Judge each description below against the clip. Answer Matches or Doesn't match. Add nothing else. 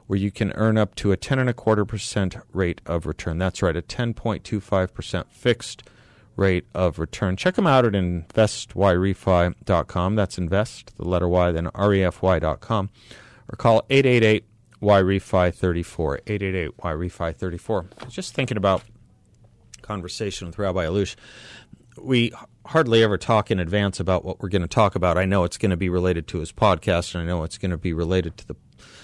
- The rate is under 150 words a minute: Doesn't match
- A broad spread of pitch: Doesn't match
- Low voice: Matches